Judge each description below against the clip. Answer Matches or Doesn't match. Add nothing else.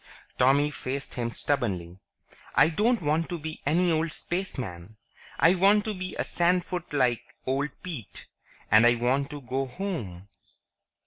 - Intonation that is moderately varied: Doesn't match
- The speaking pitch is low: Doesn't match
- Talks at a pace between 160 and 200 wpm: Doesn't match